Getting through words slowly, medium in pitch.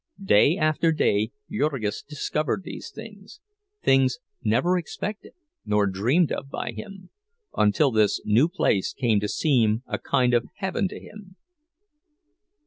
Yes: slow, 130 wpm; medium, 145 Hz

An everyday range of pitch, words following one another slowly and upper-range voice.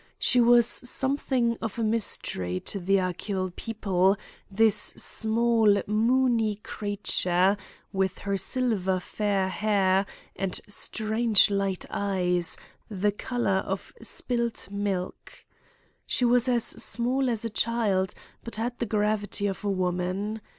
Yes: average, 3.3 semitones; slow, 120 wpm; high, 205 Hz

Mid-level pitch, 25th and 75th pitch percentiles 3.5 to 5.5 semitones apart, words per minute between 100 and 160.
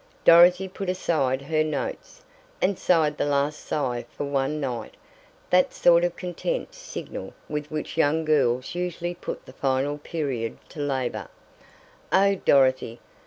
Yes: medium, 150 Hz; average, 4.4 semitones; average, 140 wpm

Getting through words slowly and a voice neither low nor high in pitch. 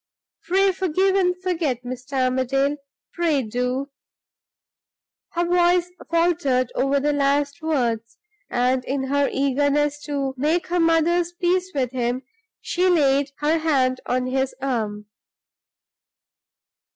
No: slow, 115 wpm; very high, 285 Hz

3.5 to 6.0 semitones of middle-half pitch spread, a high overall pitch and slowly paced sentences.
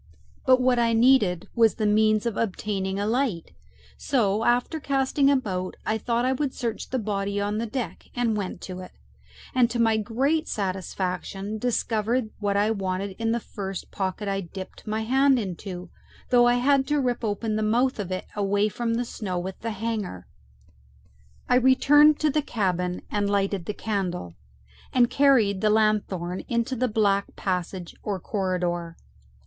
No: average, 3.9 semitones; high, 215 Hz; average, 165 wpm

